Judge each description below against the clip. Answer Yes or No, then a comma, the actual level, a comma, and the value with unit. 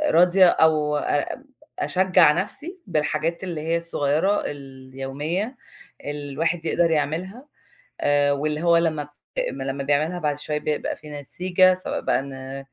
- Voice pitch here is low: No, medium, 155 Hz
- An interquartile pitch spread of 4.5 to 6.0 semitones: No, average, 3.4 semitones